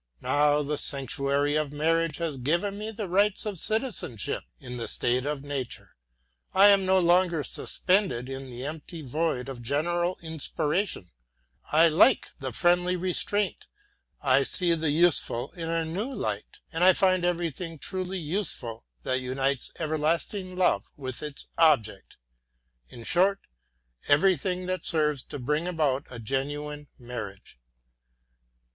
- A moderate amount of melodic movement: Yes, average, 4.8 semitones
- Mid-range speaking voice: Yes, medium, 155 Hz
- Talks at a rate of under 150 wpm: Yes, slow, 135 wpm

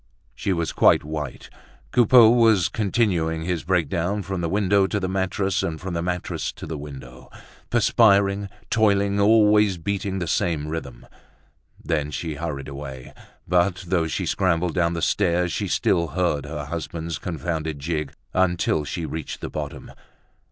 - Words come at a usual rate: Yes, average, 150 wpm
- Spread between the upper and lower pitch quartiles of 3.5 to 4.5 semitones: Yes, average, 3.8 semitones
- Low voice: Yes, very low, 85 Hz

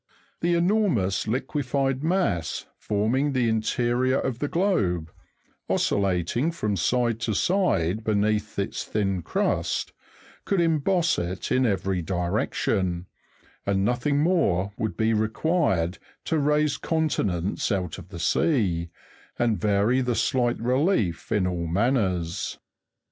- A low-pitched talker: Yes, low, 110 Hz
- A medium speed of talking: No, slow, 120 wpm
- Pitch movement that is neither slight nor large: No, wide, 6.8 semitones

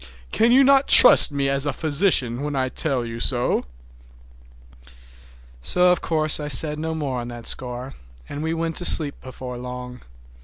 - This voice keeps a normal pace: Yes, average, 170 wpm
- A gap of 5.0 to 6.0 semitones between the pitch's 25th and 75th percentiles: No, average, 4.3 semitones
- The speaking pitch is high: No, medium, 140 Hz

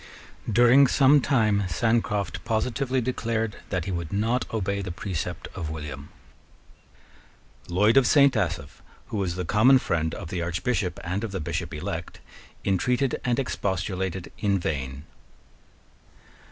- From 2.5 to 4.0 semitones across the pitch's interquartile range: No, average, 5.2 semitones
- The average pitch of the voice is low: Yes, low, 100 Hz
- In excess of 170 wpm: No, slow, 135 wpm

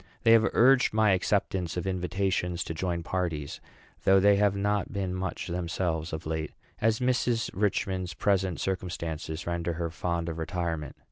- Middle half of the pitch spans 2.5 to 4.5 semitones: Yes, average, 2.9 semitones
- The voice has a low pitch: Yes, very low, 90 Hz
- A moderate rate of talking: Yes, average, 155 wpm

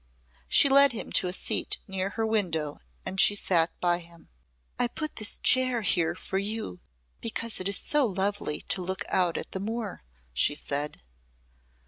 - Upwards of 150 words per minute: Yes, average, 170 wpm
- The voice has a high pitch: Yes, high, 195 Hz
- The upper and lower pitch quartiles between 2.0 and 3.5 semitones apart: No, average, 4.4 semitones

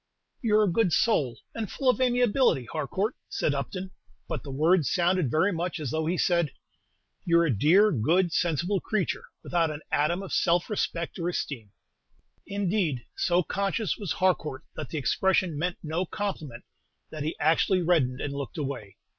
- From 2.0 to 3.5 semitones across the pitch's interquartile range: No, average, 4.1 semitones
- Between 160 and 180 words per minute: Yes, average, 165 wpm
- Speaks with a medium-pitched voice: Yes, medium, 170 Hz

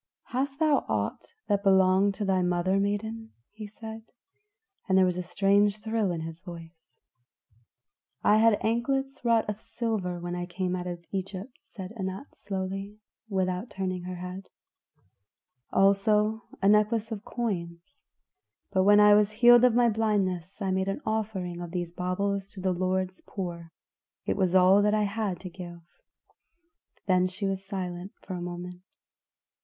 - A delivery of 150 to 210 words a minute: Yes, average, 160 wpm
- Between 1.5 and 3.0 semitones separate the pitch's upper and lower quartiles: Yes, average, 2.7 semitones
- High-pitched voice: Yes, high, 195 Hz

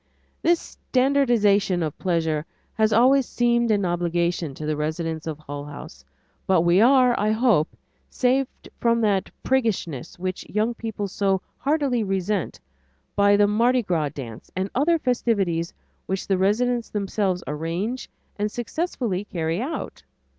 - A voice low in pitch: No, high, 200 Hz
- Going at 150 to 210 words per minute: No, average, 140 wpm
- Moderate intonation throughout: No, wide, 5.8 semitones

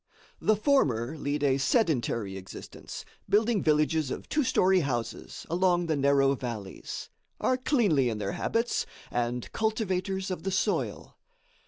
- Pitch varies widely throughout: Yes, wide, 7.7 semitones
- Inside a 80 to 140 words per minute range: Yes, slow, 135 wpm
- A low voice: No, medium, 155 Hz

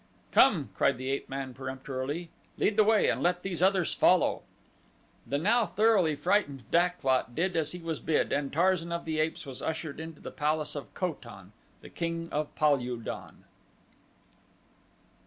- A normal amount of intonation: Yes, average, 4.4 semitones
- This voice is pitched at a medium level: Yes, medium, 160 Hz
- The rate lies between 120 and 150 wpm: No, average, 165 wpm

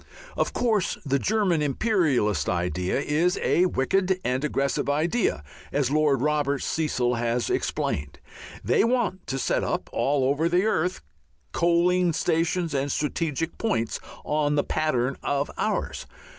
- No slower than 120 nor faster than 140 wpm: Yes, slow, 135 wpm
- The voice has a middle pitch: Yes, medium, 150 Hz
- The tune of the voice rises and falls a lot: No, average, 4.7 semitones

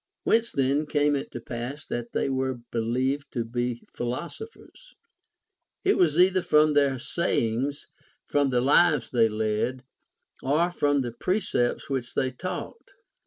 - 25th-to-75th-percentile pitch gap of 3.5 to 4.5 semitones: Yes, average, 3.8 semitones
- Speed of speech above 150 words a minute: No, average, 145 wpm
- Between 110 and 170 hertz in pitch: Yes, low, 135 Hz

